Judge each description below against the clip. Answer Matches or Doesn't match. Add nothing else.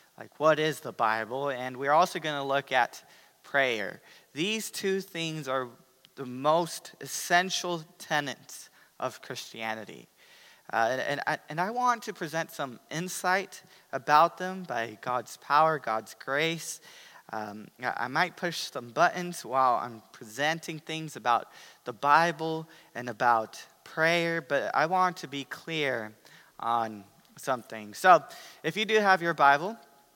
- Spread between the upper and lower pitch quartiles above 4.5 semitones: Matches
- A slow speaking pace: Doesn't match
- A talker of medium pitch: Matches